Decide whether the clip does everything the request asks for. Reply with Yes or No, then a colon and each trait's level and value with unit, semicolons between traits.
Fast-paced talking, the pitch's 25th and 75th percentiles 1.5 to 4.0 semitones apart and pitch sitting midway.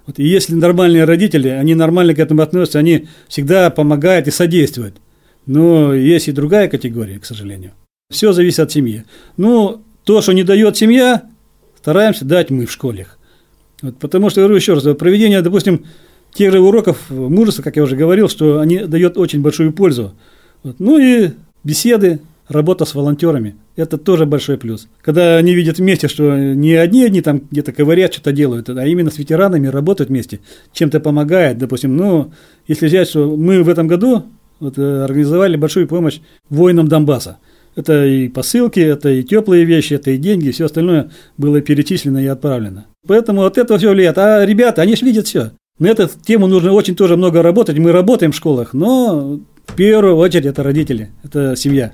No: fast, 175 wpm; average, 4.5 semitones; medium, 160 Hz